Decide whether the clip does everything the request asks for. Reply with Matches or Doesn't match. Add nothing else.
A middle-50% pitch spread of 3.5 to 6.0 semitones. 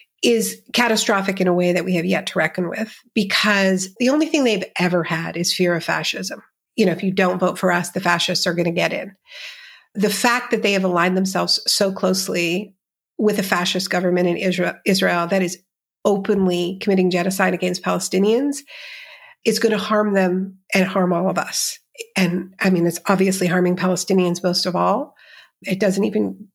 Doesn't match